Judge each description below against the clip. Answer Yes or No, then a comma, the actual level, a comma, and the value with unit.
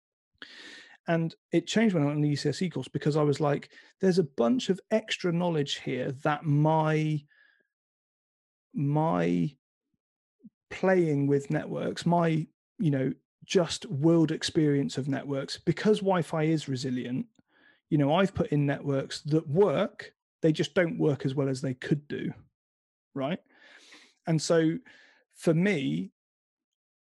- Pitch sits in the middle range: Yes, medium, 160 Hz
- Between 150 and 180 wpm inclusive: No, slow, 135 wpm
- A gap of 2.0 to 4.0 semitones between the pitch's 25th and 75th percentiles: No, average, 4.6 semitones